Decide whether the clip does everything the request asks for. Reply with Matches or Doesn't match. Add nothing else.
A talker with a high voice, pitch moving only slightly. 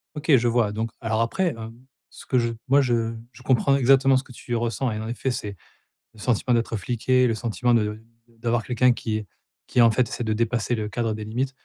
Doesn't match